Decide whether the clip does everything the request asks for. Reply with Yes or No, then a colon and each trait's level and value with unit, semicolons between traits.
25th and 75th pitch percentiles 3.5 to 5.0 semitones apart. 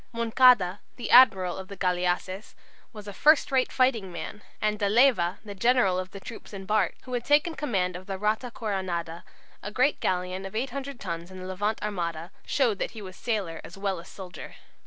Yes: average, 4.2 semitones